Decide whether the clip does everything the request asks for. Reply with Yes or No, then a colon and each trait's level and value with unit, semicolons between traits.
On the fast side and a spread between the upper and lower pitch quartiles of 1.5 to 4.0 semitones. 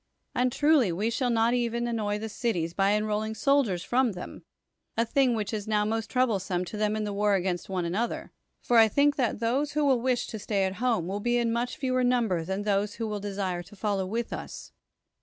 Yes: fast, 220 wpm; average, 3.3 semitones